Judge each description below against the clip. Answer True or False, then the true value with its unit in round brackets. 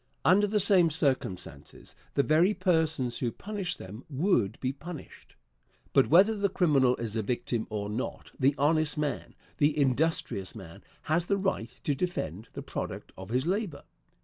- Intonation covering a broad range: True (6.8 semitones)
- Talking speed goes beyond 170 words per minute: False (160 wpm)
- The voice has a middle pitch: True (145 Hz)